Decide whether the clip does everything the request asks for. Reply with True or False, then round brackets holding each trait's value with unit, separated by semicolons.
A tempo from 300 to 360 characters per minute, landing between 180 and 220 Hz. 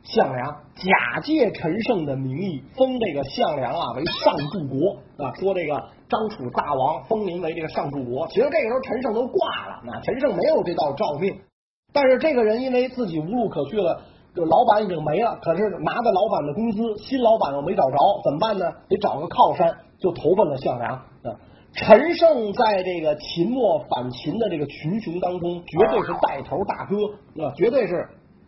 False (280 characters per minute; 185 Hz)